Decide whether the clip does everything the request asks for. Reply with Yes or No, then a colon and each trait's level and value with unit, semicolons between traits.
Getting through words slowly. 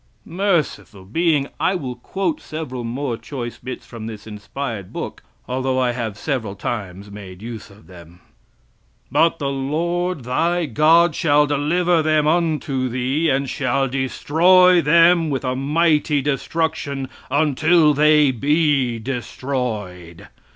Yes: slow, 130 wpm